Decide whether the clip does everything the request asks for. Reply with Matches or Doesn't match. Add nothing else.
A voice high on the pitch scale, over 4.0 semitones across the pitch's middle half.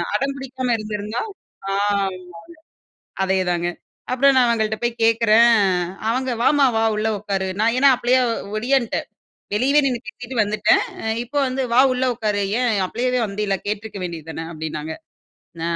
Doesn't match